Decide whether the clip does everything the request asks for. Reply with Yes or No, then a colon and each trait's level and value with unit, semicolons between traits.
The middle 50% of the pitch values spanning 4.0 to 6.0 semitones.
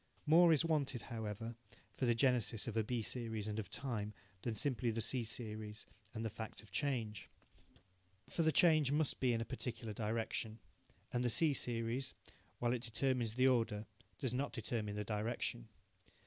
No: average, 3.0 semitones